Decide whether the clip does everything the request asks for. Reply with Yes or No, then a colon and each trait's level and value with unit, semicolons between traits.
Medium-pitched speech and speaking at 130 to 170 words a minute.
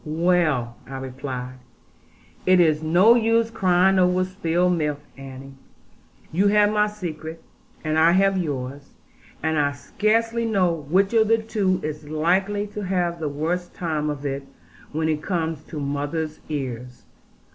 Yes: medium, 165 Hz; average, 145 wpm